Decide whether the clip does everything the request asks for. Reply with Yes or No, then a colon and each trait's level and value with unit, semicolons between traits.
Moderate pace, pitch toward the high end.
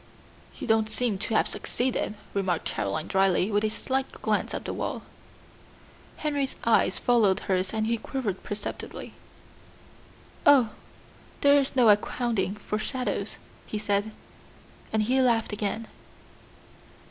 No: slow, 130 wpm; high, 220 Hz